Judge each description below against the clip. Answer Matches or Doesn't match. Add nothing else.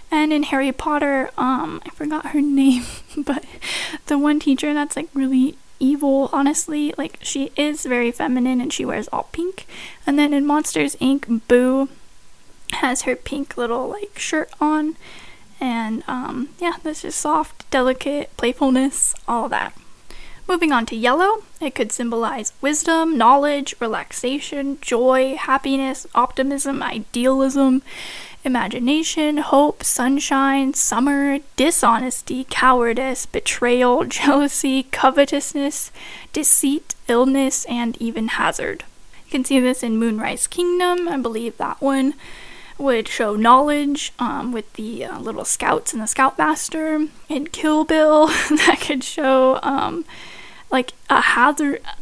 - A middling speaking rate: Doesn't match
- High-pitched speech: Matches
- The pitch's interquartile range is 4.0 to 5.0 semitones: Doesn't match